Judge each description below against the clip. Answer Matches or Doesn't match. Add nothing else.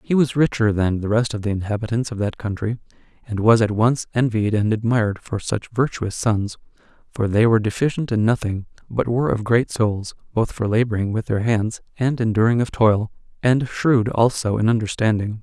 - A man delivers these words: Matches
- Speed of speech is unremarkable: Matches